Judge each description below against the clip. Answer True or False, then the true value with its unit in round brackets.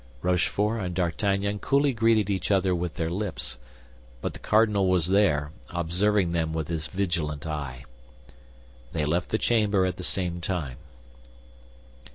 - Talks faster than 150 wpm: False (145 wpm)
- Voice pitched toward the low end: True (90 Hz)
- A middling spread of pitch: True (3.8 semitones)